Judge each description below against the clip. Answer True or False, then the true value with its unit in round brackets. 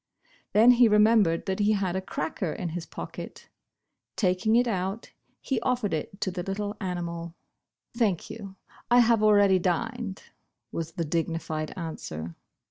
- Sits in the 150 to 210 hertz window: True (190 Hz)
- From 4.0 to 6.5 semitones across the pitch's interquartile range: True (4.3 semitones)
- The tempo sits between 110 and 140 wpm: False (150 wpm)